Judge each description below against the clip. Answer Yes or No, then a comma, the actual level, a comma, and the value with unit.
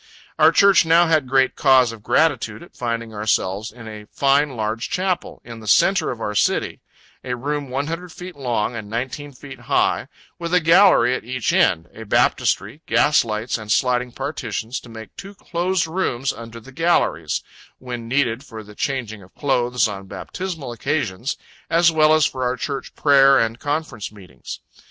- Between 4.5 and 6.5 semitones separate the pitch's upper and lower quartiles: Yes, average, 4.8 semitones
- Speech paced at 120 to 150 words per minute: No, average, 175 wpm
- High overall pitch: No, low, 125 Hz